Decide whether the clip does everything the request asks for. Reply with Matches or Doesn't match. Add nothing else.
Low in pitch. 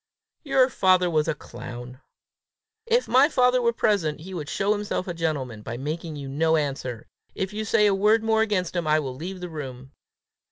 Doesn't match